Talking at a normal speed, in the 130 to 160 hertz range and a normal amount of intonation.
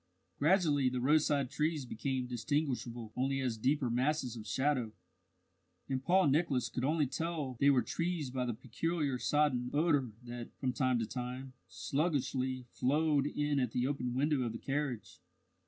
Yes: average, 155 wpm; low, 135 Hz; average, 3.1 semitones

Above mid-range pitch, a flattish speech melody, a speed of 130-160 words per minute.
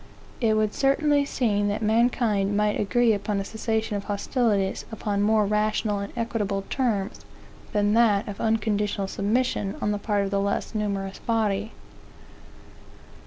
Yes: high, 210 Hz; narrow, 1.8 semitones; average, 145 wpm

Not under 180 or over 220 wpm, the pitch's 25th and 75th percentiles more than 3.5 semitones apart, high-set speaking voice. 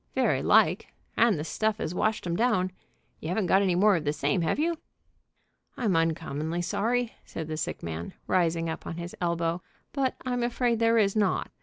No: average, 190 wpm; wide, 5.4 semitones; medium, 180 Hz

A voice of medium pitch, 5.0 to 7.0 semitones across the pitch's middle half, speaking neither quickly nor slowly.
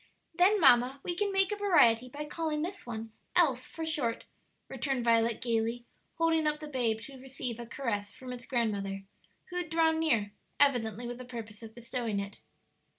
No: very high, 250 Hz; wide, 5.5 semitones; average, 180 wpm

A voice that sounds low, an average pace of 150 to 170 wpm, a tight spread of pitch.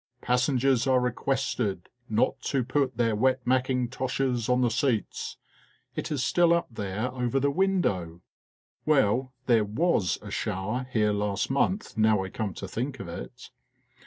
No: low, 125 Hz; average, 160 wpm; average, 3.8 semitones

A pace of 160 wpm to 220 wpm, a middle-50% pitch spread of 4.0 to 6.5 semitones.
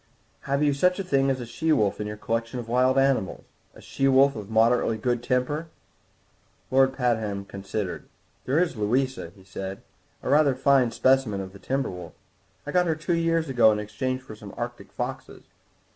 Yes: average, 190 wpm; average, 4.3 semitones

